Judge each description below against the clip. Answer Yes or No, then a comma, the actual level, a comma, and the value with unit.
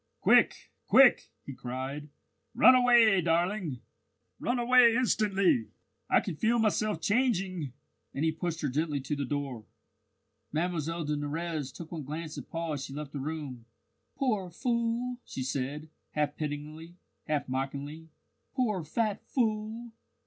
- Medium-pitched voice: Yes, medium, 165 Hz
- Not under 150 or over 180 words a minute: No, average, 140 wpm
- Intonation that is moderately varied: No, wide, 6.7 semitones